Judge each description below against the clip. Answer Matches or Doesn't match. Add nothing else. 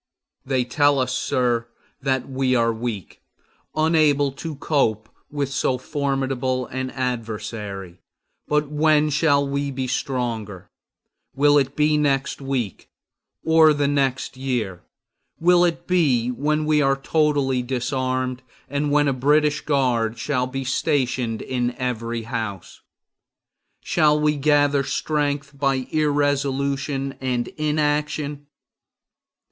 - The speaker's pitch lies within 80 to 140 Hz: Matches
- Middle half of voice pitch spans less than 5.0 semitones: Matches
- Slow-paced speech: Matches